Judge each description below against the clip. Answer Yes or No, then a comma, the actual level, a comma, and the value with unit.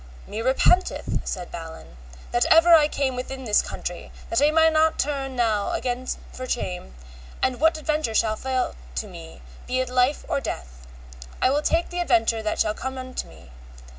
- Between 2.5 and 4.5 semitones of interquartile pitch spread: No, average, 5.2 semitones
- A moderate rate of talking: Yes, average, 180 wpm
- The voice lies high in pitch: Yes, very high, 255 Hz